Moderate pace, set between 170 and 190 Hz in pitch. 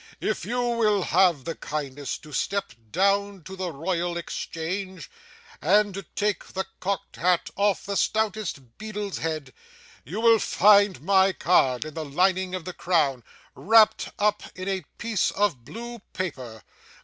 Yes: average, 150 wpm; medium, 185 Hz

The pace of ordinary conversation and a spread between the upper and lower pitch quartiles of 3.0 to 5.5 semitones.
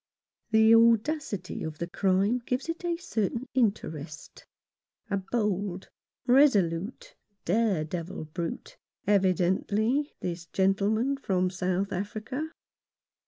No: slow, 100 wpm; average, 4.9 semitones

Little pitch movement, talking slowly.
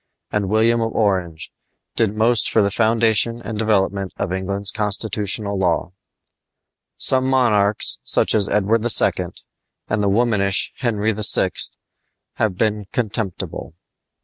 Yes: narrow, 2.3 semitones; slow, 120 wpm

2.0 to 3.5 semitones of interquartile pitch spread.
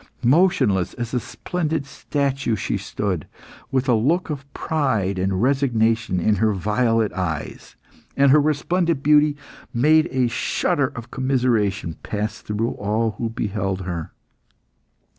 No: average, 5.3 semitones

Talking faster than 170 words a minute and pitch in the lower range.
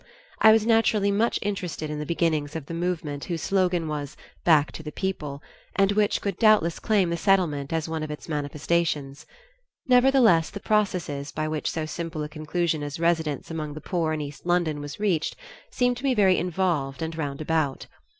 No: average, 185 wpm; medium, 165 Hz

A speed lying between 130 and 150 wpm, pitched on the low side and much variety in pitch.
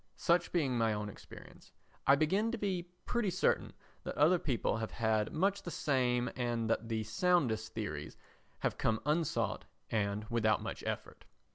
No: average, 160 wpm; low, 125 Hz; wide, 7.8 semitones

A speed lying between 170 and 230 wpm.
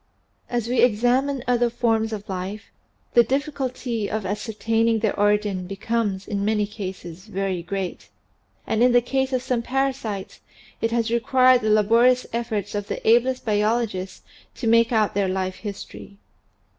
No: average, 155 wpm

